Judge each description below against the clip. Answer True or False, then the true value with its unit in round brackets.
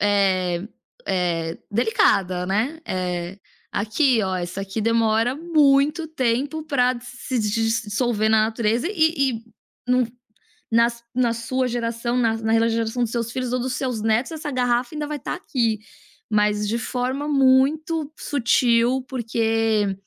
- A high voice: True (235 Hz)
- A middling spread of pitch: True (3.3 semitones)